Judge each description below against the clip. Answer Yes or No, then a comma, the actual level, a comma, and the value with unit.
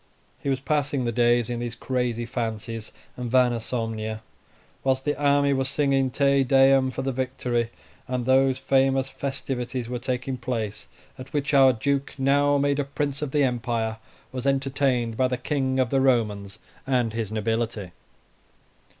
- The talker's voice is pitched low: Yes, low, 130 Hz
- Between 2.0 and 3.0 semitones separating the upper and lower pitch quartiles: Yes, narrow, 2.4 semitones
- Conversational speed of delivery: Yes, average, 160 wpm